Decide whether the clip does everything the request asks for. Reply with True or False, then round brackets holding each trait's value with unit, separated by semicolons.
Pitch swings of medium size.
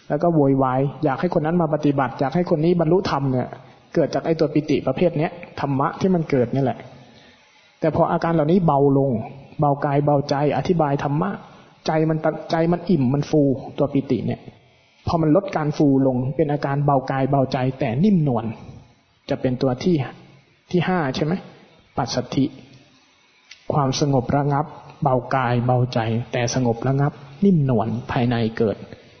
True (3.6 semitones)